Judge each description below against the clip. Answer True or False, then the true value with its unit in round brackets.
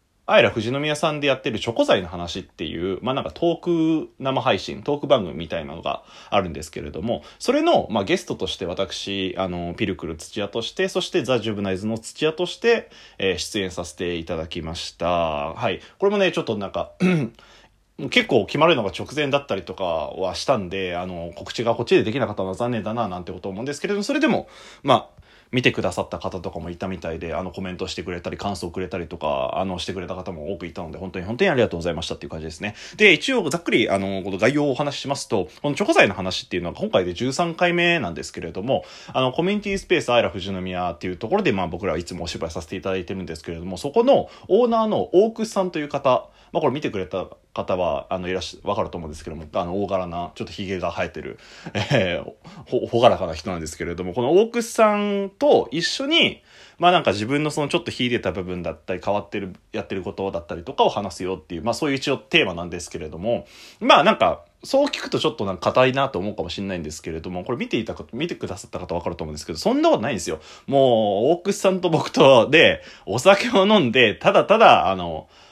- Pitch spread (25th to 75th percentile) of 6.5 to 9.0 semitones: True (8.4 semitones)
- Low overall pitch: True (100 Hz)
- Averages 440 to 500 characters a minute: True (490 characters per minute)